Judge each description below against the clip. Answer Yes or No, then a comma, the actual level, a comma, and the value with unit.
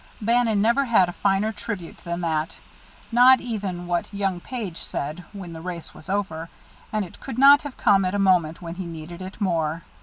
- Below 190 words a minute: No, average, 195 wpm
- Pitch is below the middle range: No, high, 190 Hz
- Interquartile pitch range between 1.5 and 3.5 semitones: No, average, 4.0 semitones